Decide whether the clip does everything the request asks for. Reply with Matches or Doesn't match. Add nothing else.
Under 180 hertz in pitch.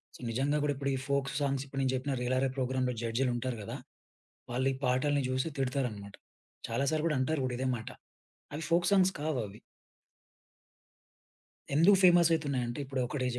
Matches